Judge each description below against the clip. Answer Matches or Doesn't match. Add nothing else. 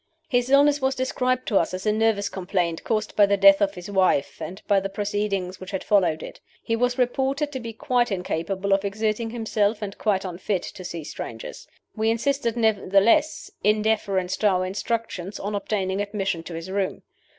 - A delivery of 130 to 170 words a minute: Doesn't match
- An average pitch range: Matches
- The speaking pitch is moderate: Doesn't match